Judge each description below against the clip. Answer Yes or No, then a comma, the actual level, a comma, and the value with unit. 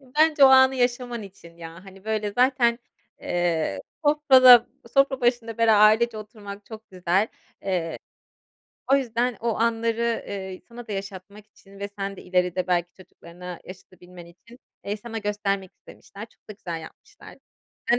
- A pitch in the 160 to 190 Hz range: No, high, 210 Hz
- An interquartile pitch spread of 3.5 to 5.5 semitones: Yes, average, 4.3 semitones